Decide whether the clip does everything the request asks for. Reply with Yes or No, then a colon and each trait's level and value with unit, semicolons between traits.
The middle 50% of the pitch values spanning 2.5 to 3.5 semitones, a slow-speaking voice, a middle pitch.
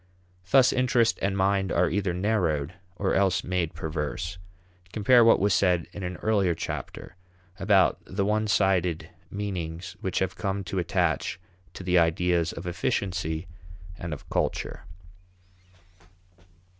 No: average, 2.8 semitones; slow, 130 wpm; very low, 90 Hz